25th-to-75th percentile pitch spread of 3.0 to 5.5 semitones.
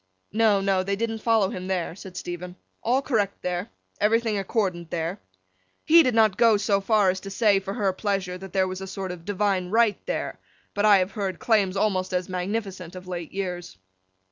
No: narrow, 2.6 semitones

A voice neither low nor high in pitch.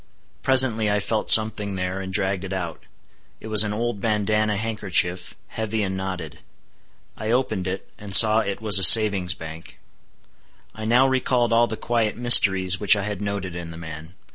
No: low, 105 Hz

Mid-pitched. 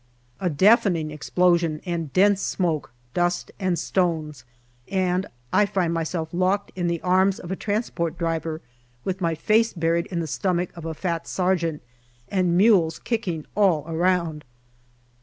Yes: medium, 175 Hz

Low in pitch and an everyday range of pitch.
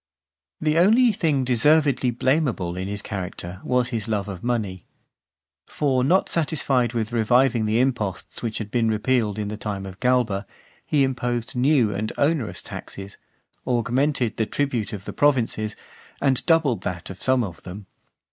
Yes: low, 120 Hz; average, 4.3 semitones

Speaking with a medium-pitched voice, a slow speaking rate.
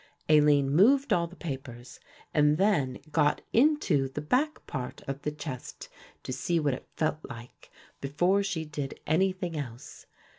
No: medium, 150 Hz; average, 150 wpm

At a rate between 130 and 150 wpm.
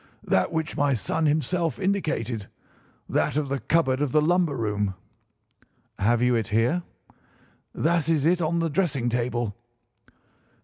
Yes: slow, 135 wpm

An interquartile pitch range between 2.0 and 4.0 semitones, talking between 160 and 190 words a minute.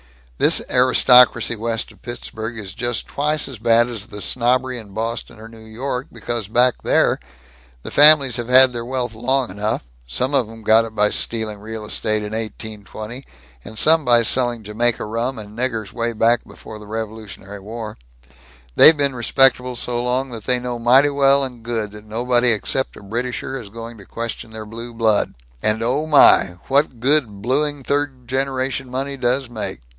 Yes: average, 2.7 semitones; average, 180 wpm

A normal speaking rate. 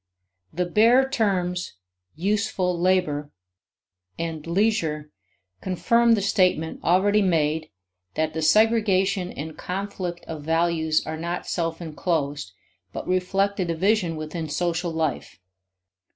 No: slow, 110 wpm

